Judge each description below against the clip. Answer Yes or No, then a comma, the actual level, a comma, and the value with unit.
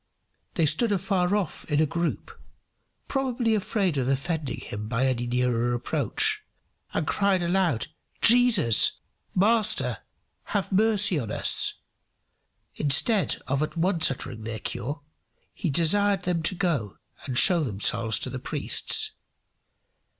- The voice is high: No, medium, 165 Hz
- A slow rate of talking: Yes, slow, 130 wpm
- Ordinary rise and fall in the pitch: No, wide, 7.5 semitones